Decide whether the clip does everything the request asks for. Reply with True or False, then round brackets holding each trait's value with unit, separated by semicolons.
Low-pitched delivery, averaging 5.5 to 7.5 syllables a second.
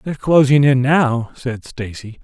False (130 Hz; 4.4 syllables/s)